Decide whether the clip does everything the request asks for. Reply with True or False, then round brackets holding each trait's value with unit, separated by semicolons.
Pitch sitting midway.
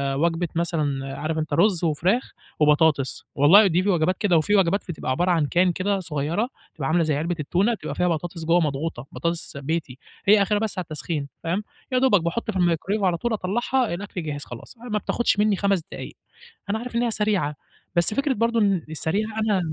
True (175 Hz)